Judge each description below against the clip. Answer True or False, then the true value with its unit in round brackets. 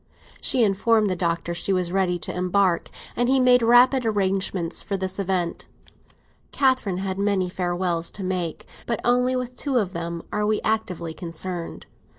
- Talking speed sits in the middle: True (165 wpm)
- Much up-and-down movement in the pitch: False (4.3 semitones)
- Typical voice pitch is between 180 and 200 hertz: True (190 Hz)